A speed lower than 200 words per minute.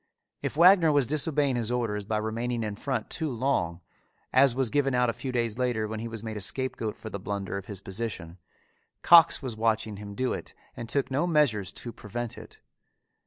No: fast, 205 wpm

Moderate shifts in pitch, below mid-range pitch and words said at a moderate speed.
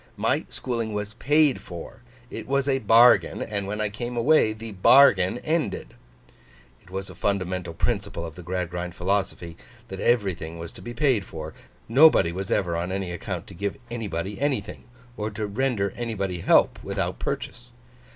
Yes: average, 4.7 semitones; low, 100 Hz; average, 160 wpm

